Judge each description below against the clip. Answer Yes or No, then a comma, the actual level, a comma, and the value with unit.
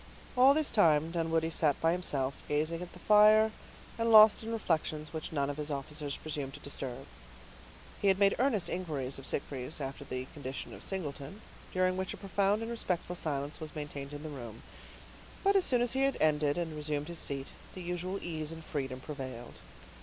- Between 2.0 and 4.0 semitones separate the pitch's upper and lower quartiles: No, average, 5.1 semitones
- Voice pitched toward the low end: No, medium, 160 Hz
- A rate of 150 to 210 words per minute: Yes, average, 190 wpm